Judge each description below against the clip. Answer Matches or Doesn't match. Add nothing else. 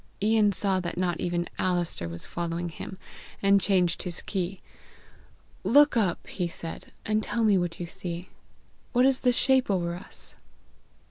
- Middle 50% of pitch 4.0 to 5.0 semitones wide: Doesn't match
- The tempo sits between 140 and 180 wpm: Matches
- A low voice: Doesn't match